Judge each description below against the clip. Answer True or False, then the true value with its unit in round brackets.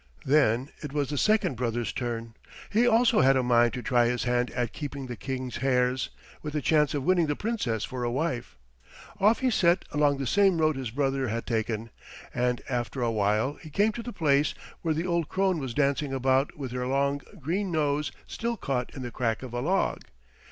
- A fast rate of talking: True (210 wpm)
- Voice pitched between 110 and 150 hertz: True (135 Hz)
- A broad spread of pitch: False (4.3 semitones)